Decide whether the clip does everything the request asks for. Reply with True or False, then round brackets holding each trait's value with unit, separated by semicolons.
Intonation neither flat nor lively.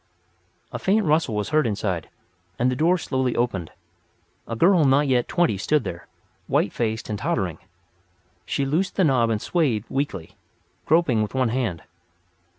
False (6.1 semitones)